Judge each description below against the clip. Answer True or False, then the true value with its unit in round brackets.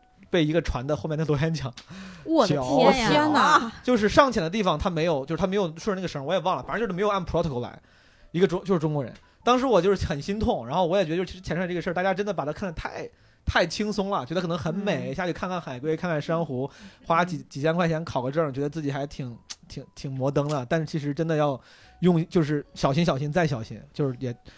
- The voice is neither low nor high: True (170 Hz)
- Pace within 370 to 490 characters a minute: True (375 characters per minute)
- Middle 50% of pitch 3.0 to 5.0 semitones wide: True (4.1 semitones)